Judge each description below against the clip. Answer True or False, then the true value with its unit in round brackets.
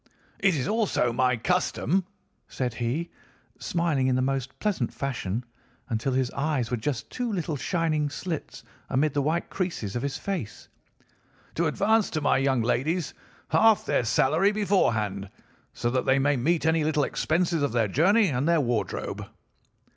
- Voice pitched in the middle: True (145 Hz)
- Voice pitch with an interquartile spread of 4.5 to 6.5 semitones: True (5.5 semitones)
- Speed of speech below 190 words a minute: True (160 wpm)